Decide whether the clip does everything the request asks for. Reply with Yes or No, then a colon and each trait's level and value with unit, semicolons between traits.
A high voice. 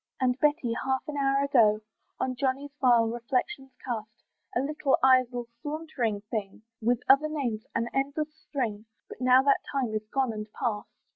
Yes: very high, 255 Hz